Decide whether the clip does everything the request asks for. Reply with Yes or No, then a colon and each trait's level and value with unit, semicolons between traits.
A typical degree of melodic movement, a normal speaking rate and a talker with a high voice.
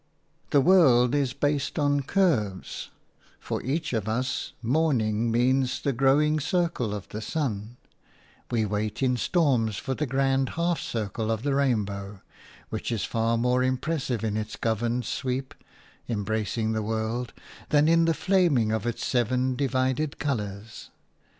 No: average, 4.2 semitones; average, 150 wpm; low, 125 Hz